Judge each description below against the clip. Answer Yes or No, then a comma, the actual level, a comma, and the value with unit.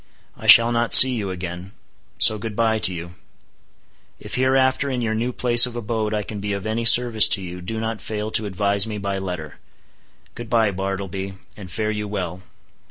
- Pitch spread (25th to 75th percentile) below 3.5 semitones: Yes, average, 3.1 semitones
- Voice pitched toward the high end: No, low, 105 Hz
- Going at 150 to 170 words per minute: No, average, 195 wpm